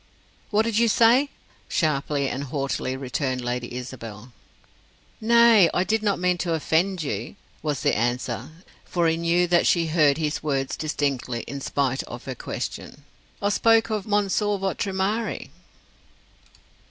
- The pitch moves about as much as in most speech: No, wide, 7.1 semitones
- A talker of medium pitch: Yes, medium, 160 Hz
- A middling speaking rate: Yes, average, 145 wpm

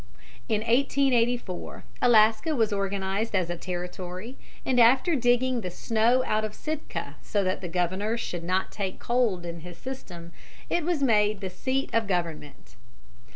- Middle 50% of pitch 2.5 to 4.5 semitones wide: No, average, 5.2 semitones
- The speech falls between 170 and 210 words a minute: No, average, 155 wpm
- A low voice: No, high, 215 Hz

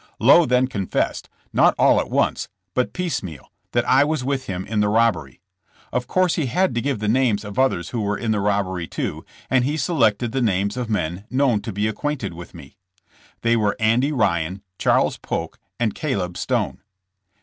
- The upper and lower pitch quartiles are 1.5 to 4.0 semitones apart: No, average, 4.6 semitones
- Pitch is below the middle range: Yes, low, 115 Hz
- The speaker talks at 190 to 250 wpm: Yes, average, 195 wpm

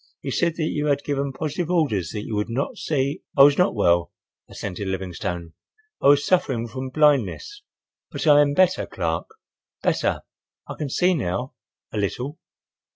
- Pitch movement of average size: No, wide, 6.5 semitones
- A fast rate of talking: No, average, 160 wpm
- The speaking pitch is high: No, low, 135 Hz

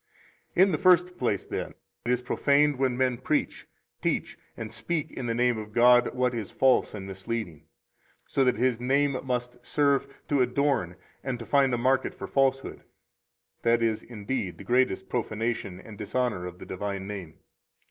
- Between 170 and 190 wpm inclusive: Yes, average, 175 wpm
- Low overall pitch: Yes, low, 125 Hz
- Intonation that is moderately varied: Yes, average, 3.7 semitones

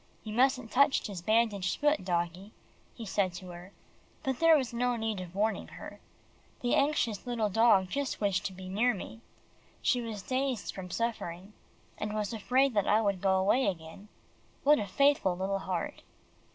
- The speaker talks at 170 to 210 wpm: Yes, average, 175 wpm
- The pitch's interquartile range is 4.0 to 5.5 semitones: Yes, average, 4.6 semitones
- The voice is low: No, high, 210 Hz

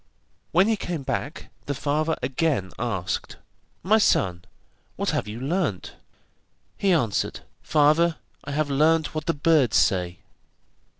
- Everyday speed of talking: No, slow, 130 wpm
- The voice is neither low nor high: Yes, medium, 150 Hz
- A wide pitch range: Yes, wide, 5.7 semitones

